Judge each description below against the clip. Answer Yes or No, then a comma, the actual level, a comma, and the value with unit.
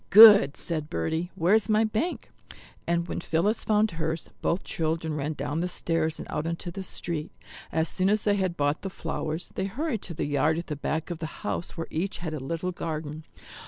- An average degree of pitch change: Yes, average, 3.4 semitones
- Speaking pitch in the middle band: Yes, medium, 165 Hz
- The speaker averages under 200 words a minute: No, fast, 205 wpm